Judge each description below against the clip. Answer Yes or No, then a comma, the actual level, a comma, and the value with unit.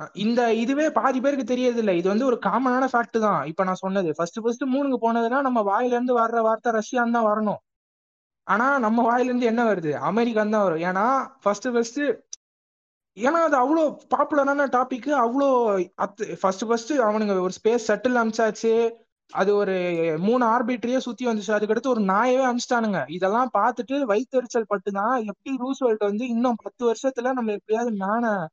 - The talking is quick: Yes, fast, 150 wpm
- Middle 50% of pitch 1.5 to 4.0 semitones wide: Yes, average, 3.7 semitones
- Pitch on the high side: Yes, high, 230 Hz